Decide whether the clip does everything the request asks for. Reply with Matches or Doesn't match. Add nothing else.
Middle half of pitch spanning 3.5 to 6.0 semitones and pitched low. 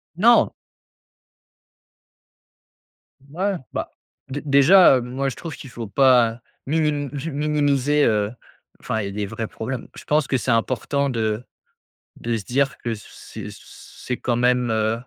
Matches